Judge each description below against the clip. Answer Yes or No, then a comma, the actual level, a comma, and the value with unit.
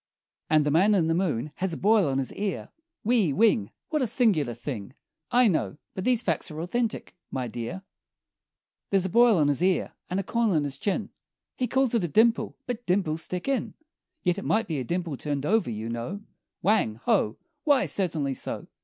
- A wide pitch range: Yes, wide, 7.1 semitones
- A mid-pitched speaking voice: Yes, medium, 180 Hz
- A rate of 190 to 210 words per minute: Yes, average, 200 wpm